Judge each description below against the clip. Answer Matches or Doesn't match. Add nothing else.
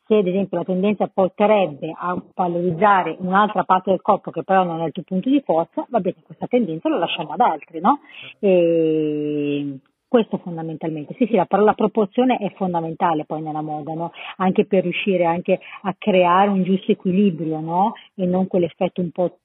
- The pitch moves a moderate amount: Matches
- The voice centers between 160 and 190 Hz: Matches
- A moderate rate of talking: Doesn't match